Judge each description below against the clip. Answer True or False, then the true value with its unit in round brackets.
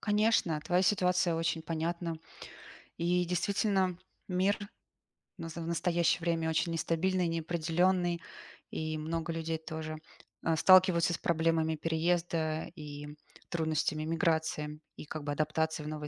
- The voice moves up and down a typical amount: False (1.8 semitones)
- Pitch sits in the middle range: True (165 Hz)